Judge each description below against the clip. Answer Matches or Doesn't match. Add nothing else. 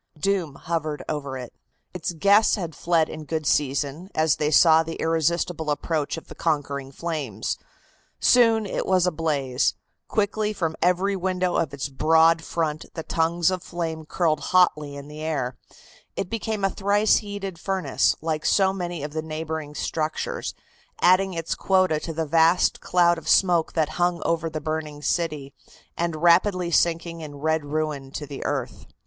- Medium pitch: Matches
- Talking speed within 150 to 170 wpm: Matches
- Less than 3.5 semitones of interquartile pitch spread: Matches